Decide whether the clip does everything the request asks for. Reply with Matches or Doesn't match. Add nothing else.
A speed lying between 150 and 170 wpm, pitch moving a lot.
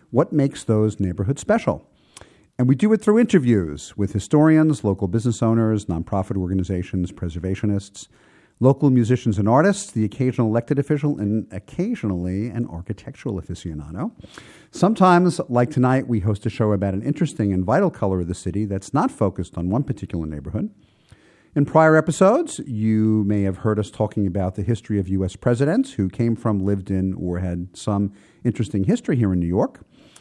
Matches